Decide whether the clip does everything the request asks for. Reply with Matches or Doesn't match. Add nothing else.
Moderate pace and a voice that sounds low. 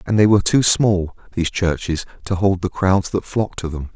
Doesn't match